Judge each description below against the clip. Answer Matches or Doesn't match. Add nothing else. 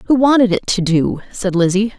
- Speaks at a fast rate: Matches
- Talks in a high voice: Matches